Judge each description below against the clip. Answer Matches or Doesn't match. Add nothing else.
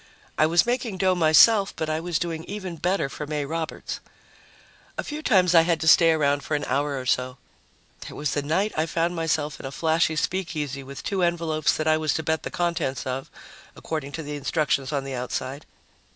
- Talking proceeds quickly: Matches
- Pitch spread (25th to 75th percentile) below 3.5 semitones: Matches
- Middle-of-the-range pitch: Matches